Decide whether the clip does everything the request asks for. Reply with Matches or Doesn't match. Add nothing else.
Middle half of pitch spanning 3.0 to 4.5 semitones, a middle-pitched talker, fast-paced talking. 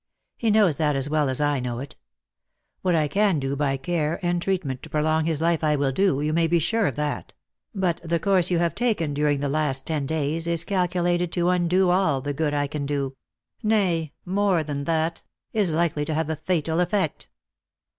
Matches